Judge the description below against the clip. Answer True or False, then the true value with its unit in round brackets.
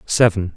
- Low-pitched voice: True (100 Hz)